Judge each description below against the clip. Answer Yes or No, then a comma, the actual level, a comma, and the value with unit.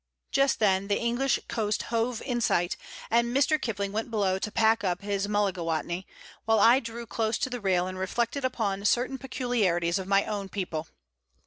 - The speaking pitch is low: No, high, 210 Hz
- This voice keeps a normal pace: Yes, average, 180 wpm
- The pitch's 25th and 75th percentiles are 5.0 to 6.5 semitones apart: No, average, 3.7 semitones